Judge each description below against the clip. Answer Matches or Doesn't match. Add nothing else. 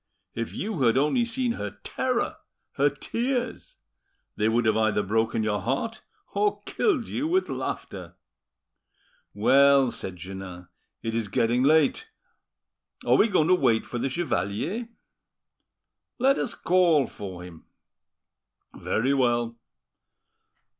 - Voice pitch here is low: Matches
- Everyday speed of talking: Doesn't match